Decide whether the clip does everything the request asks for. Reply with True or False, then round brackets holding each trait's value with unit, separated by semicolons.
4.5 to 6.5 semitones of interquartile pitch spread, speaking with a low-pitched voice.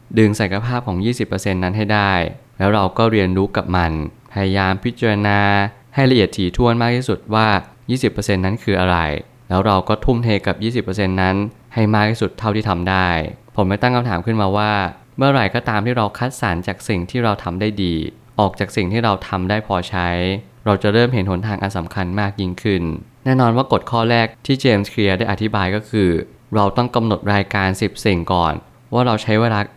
False (3.4 semitones; 105 Hz)